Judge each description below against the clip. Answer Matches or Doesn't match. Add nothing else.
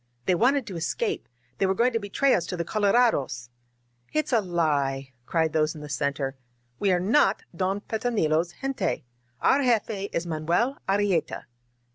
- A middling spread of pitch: Doesn't match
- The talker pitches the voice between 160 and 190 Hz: Matches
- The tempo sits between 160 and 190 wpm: Matches